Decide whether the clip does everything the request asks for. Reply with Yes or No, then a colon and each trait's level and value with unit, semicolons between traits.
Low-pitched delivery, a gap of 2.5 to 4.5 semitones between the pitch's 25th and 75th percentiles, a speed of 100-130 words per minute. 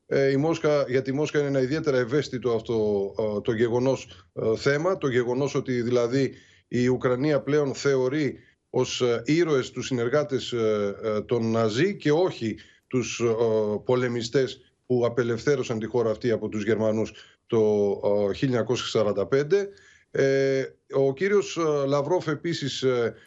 Yes: low, 125 Hz; average, 3.9 semitones; slow, 115 wpm